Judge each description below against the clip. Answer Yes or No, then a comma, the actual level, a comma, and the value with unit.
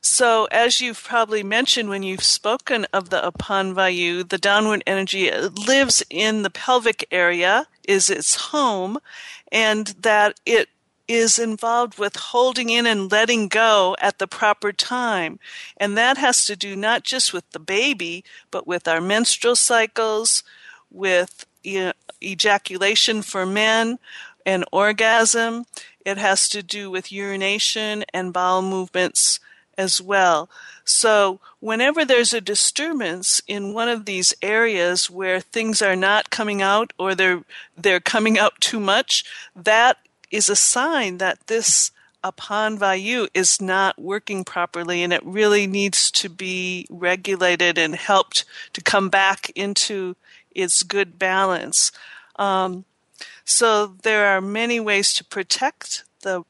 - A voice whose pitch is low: No, high, 205 Hz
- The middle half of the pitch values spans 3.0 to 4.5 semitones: Yes, average, 3.3 semitones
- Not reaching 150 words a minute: Yes, average, 140 wpm